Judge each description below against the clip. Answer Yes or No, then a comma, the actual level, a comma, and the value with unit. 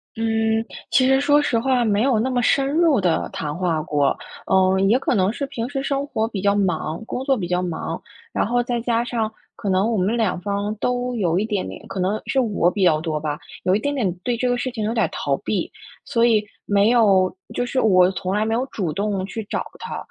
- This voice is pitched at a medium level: No, high, 215 Hz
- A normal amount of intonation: Yes, average, 4.7 semitones